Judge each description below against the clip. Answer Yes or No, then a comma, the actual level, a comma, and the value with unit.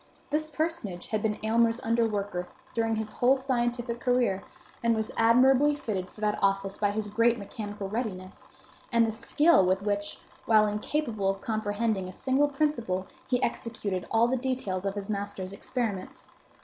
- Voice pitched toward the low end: No, high, 220 Hz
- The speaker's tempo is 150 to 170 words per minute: Yes, average, 160 wpm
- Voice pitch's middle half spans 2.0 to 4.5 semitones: Yes, average, 3.4 semitones